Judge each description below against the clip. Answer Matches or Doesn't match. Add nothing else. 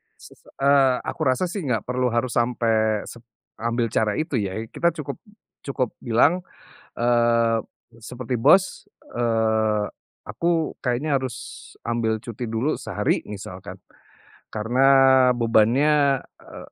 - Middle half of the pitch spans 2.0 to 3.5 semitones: Matches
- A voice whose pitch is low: Matches